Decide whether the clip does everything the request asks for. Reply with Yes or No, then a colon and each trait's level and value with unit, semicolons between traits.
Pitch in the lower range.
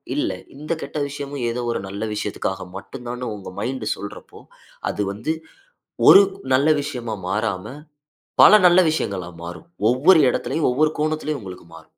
Yes: low, 125 Hz